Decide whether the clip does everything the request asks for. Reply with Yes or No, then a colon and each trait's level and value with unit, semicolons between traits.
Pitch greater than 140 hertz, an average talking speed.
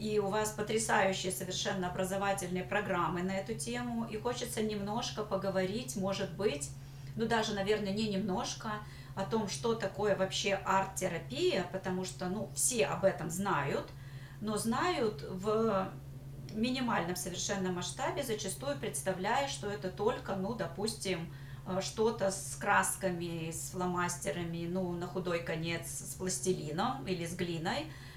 Yes: high, 190 Hz; average, 130 wpm